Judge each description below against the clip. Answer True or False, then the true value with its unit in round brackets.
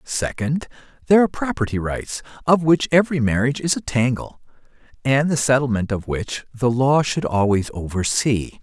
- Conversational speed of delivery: True (155 wpm)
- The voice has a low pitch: True (130 Hz)